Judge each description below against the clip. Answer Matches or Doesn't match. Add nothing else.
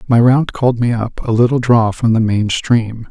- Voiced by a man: Matches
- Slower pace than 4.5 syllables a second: Doesn't match